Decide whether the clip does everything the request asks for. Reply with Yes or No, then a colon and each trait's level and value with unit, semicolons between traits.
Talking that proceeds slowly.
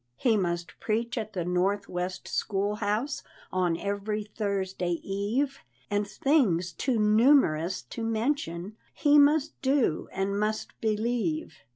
Yes: slow, 130 wpm